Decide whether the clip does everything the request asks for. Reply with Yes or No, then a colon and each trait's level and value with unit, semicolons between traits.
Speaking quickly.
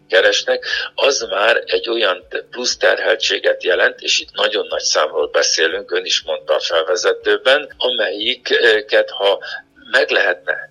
No: average, 130 wpm